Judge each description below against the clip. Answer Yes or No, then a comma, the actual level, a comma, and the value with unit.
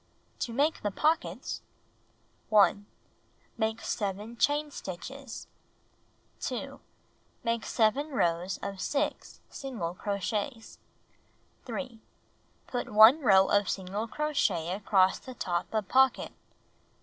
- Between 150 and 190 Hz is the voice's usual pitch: No, high, 220 Hz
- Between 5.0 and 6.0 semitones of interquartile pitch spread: Yes, average, 5.3 semitones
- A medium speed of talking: No, slow, 100 wpm